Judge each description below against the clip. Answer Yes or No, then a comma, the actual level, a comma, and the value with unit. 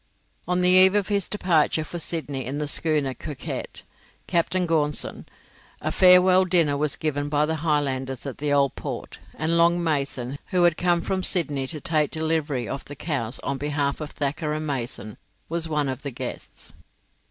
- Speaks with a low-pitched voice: No, medium, 150 Hz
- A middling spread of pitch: Yes, average, 3.3 semitones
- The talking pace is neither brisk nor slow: Yes, average, 175 wpm